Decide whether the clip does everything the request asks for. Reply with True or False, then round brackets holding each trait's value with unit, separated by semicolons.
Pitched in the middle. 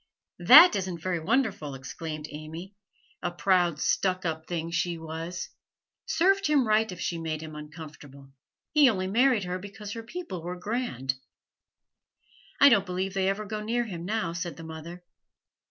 True (180 Hz)